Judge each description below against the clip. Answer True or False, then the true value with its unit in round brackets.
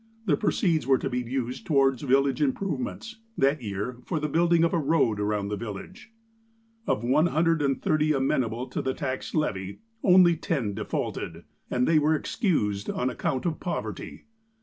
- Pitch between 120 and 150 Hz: True (135 Hz)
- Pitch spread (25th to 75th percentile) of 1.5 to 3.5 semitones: False (4.8 semitones)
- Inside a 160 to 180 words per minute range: True (170 wpm)